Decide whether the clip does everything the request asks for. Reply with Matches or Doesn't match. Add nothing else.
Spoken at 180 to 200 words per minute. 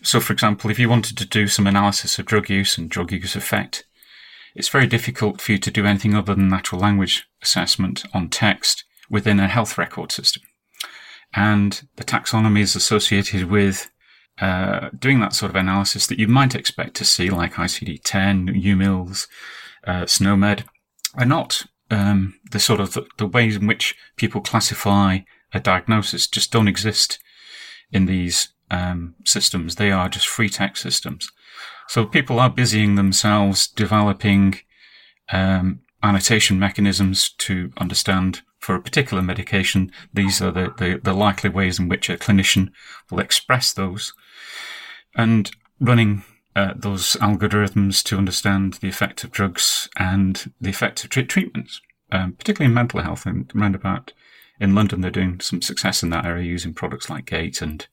Doesn't match